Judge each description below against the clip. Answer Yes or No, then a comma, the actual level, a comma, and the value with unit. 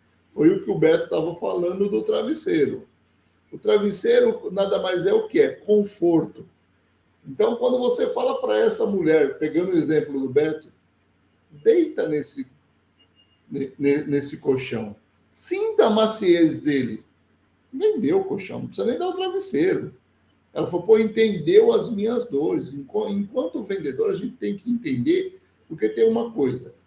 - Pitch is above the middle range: Yes, high, 210 Hz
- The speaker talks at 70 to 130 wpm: No, average, 145 wpm